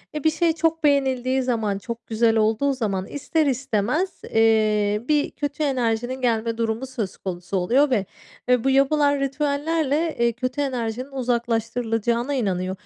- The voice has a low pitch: No, very high, 250 Hz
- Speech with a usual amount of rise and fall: Yes, average, 4.1 semitones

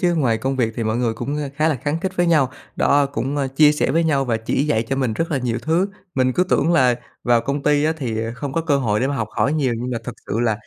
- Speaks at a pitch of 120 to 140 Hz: Yes, low, 135 Hz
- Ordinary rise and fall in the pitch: Yes, average, 3.9 semitones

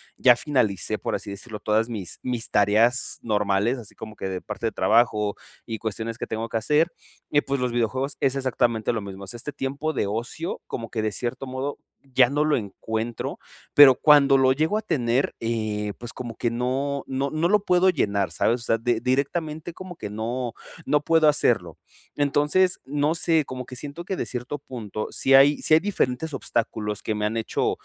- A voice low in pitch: Yes, low, 125 Hz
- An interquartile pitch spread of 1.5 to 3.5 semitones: No, average, 4.6 semitones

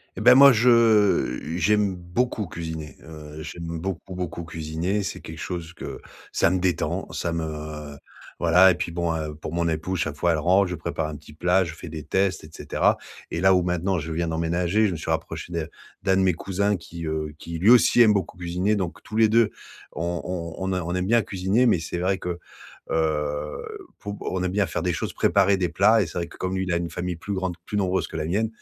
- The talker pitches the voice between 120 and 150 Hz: No, very low, 90 Hz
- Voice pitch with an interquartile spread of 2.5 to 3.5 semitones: Yes, average, 2.9 semitones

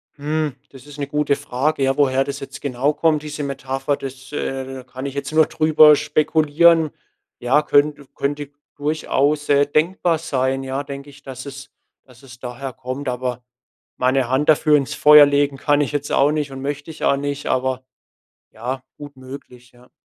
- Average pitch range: No, narrow, 2.0 semitones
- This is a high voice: No, medium, 140 Hz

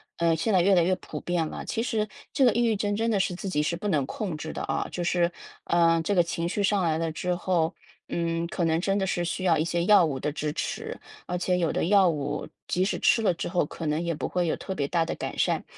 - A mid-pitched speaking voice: Yes, medium, 175 Hz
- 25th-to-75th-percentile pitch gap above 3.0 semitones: No, average, 2.7 semitones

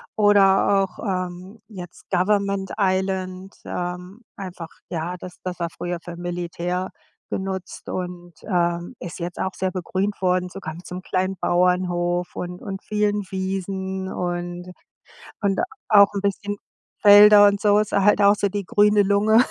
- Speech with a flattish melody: Yes, narrow, 2.1 semitones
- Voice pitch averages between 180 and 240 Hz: Yes, high, 190 Hz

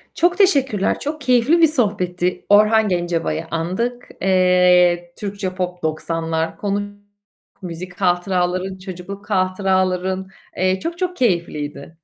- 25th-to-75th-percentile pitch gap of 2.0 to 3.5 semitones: Yes, average, 3.0 semitones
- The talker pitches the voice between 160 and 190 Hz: Yes, medium, 185 Hz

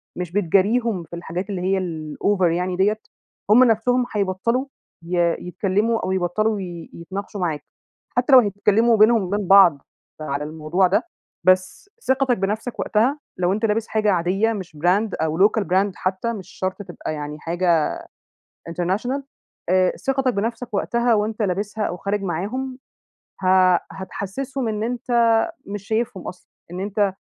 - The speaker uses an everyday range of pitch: Yes, average, 3.7 semitones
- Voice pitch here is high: Yes, high, 200 Hz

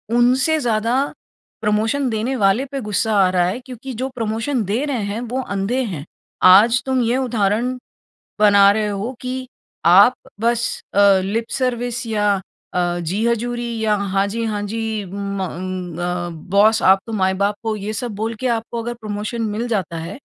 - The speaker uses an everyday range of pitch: Yes, average, 3.3 semitones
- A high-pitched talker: Yes, high, 220 Hz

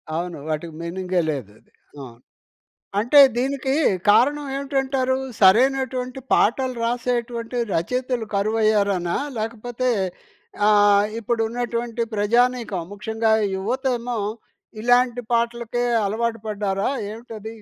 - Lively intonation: No, average, 3.4 semitones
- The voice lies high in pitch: Yes, high, 230 Hz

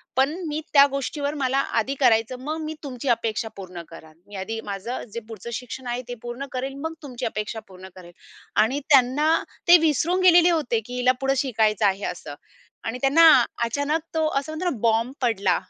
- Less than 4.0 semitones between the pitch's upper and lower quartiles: No, average, 4.4 semitones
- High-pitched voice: Yes, very high, 250 Hz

